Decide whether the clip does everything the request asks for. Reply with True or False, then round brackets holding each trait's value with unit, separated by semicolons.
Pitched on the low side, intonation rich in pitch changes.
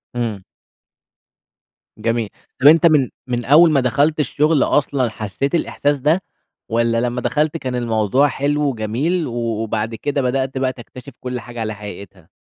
False (125 Hz; 4.1 semitones)